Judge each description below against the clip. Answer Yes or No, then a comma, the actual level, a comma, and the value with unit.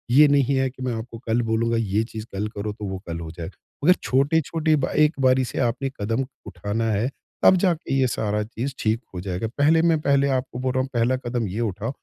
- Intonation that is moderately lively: Yes, average, 4.4 semitones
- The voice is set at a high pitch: No, low, 120 Hz